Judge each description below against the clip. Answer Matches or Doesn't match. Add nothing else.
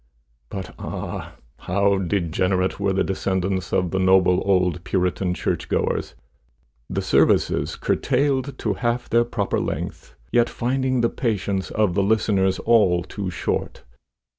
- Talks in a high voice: Doesn't match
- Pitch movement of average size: Matches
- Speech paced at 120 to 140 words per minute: Matches